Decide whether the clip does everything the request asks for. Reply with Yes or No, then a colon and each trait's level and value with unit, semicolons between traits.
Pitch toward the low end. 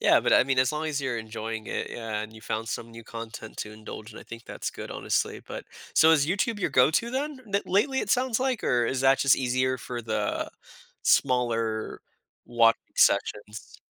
Yes: low, 125 Hz